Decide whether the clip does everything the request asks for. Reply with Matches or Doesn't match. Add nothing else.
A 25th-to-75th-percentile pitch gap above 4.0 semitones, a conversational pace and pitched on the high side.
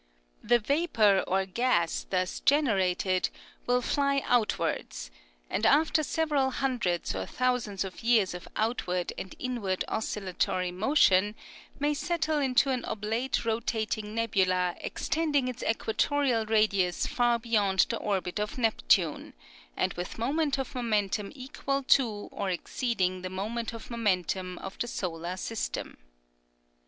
Doesn't match